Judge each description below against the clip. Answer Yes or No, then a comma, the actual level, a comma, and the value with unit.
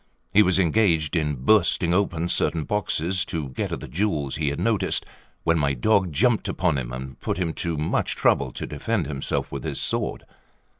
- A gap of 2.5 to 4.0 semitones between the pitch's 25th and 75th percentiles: No, average, 5.0 semitones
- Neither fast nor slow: Yes, average, 190 wpm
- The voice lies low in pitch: Yes, very low, 85 Hz